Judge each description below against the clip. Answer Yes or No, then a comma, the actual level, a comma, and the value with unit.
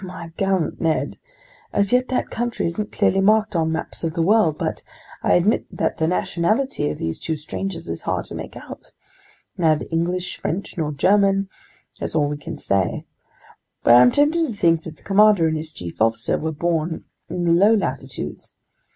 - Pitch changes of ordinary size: Yes, average, 4.2 semitones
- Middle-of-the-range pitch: Yes, medium, 170 Hz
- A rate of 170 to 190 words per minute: Yes, average, 185 wpm